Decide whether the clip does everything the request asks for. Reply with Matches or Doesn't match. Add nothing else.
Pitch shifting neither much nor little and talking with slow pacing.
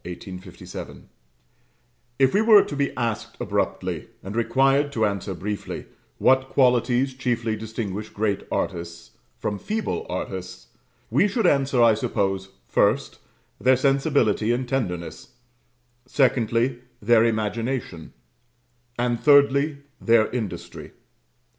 Matches